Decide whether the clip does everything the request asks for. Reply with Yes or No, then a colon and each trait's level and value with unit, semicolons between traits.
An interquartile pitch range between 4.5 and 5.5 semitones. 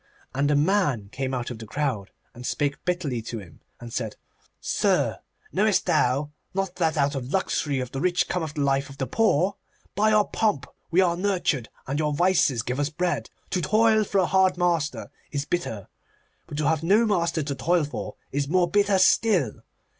Yes: average, 5.2 semitones